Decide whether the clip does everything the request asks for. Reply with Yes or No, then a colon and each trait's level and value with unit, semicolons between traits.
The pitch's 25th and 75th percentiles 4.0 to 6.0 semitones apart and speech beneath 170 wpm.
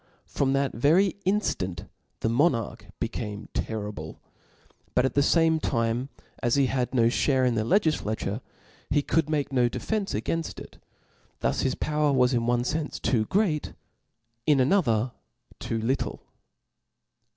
Yes: average, 4.7 semitones; average, 140 wpm